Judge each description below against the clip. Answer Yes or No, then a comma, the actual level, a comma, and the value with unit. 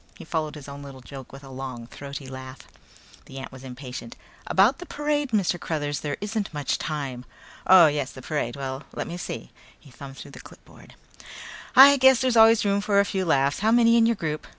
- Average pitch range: No, wide, 7.4 semitones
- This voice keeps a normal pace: No, fast, 210 wpm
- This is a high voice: No, medium, 150 Hz